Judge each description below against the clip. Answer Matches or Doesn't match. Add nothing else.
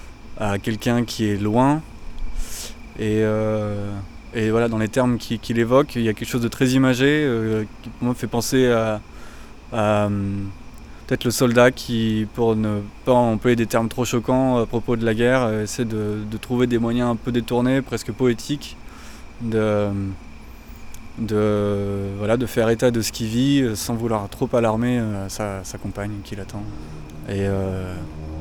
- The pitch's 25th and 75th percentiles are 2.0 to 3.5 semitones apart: Matches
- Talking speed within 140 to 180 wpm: Matches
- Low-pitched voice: Matches